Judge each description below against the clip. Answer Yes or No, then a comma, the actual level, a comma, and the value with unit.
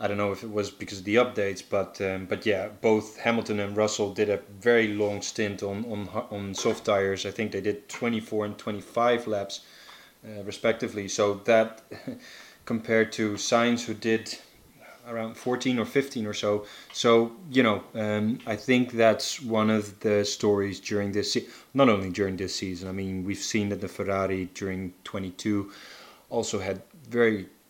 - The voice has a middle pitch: No, low, 105 Hz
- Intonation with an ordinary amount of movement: No, narrow, 2.1 semitones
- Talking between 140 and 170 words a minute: No, average, 180 wpm